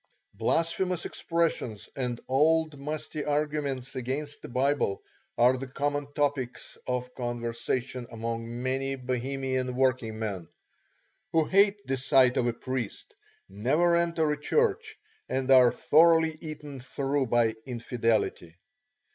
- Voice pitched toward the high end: No, low, 135 Hz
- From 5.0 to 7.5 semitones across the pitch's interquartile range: No, average, 3.6 semitones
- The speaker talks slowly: Yes, slow, 120 wpm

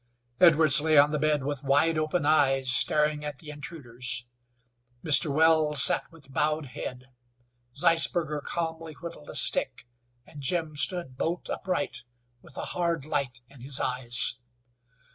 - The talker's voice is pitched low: No, medium, 150 Hz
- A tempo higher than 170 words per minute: No, average, 145 wpm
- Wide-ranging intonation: No, average, 3.1 semitones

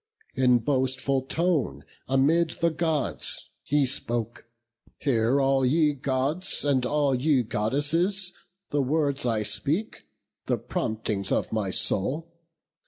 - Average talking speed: No, slow, 115 wpm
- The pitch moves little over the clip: No, average, 3.7 semitones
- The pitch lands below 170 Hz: Yes, low, 135 Hz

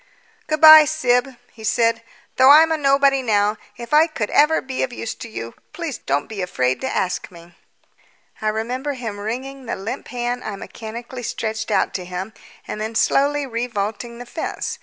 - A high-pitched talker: Yes, high, 235 Hz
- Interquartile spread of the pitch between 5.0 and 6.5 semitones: No, average, 4.1 semitones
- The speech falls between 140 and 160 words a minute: No, average, 180 wpm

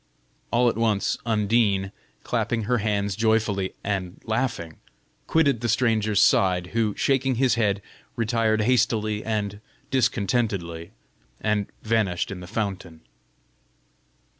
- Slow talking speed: Yes, slow, 115 wpm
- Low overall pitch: Yes, low, 110 Hz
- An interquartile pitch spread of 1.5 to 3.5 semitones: Yes, average, 2.8 semitones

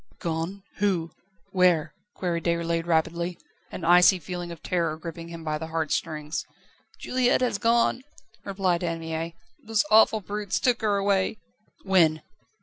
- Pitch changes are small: No, average, 3.3 semitones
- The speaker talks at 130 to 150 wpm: Yes, average, 145 wpm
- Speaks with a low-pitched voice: No, medium, 175 Hz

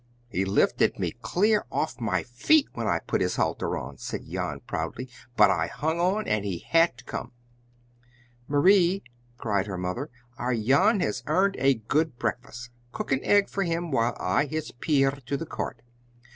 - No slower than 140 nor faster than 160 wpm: No, average, 175 wpm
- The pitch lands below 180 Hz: Yes, low, 135 Hz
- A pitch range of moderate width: No, wide, 7.0 semitones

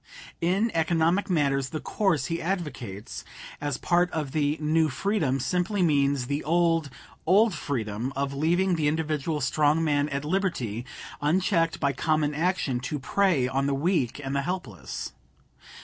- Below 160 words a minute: Yes, average, 150 wpm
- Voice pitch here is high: No, medium, 155 Hz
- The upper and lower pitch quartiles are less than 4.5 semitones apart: Yes, average, 3.9 semitones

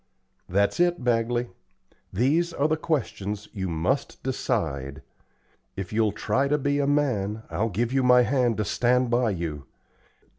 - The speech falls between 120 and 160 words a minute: Yes, average, 150 wpm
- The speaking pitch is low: Yes, low, 120 Hz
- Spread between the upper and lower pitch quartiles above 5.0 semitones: Yes, wide, 5.4 semitones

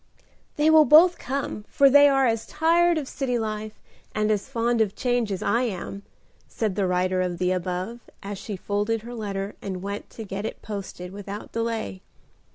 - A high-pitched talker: Yes, high, 215 Hz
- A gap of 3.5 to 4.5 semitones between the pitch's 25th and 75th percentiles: Yes, average, 4.0 semitones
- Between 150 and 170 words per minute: No, average, 185 wpm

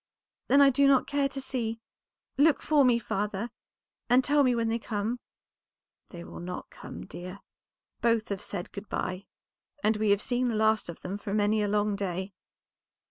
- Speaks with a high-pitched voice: Yes, high, 220 Hz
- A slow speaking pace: No, average, 185 wpm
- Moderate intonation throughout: Yes, average, 3.8 semitones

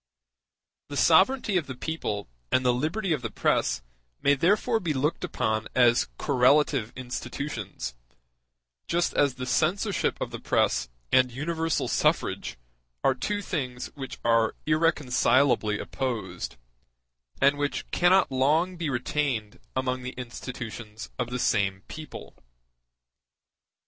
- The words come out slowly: Yes, slow, 125 wpm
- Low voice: Yes, low, 130 Hz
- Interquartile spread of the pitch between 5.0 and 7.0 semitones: No, average, 4.6 semitones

